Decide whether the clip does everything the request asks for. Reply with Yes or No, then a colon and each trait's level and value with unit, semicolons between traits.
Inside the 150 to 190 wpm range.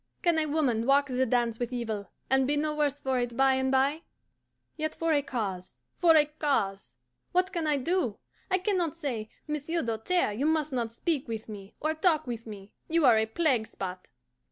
No: fast, 205 wpm